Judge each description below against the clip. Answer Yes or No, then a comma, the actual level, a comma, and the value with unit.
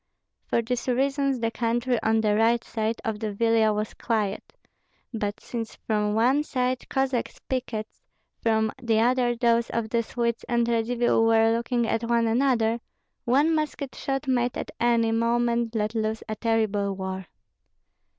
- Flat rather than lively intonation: Yes, narrow, 1.7 semitones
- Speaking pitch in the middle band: No, high, 230 Hz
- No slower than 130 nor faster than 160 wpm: Yes, average, 155 wpm